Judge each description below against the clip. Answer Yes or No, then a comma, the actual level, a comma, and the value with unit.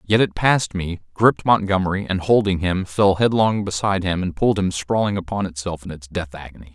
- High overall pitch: No, very low, 95 Hz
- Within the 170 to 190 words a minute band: No, fast, 205 wpm